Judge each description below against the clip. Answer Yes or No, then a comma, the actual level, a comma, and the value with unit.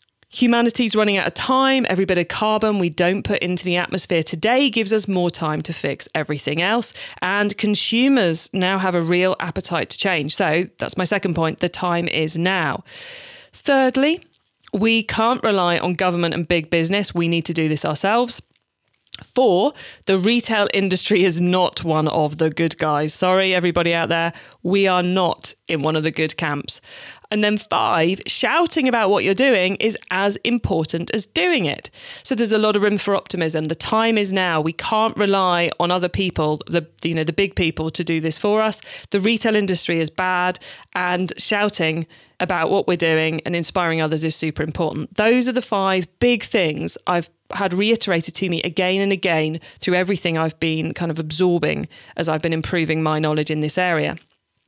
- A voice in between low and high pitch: Yes, medium, 180 Hz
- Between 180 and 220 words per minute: Yes, average, 190 wpm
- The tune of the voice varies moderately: Yes, average, 4.1 semitones